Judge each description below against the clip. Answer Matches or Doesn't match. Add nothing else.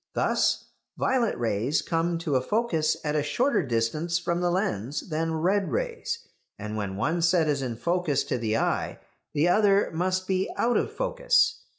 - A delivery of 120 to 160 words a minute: Doesn't match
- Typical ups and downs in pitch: Doesn't match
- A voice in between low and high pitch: Matches